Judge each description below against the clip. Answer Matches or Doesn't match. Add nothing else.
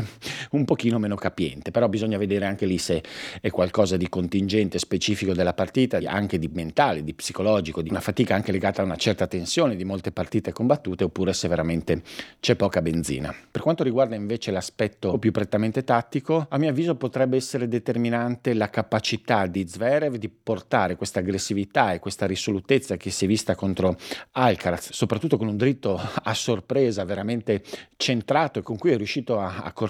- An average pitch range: Matches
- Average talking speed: Doesn't match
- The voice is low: Matches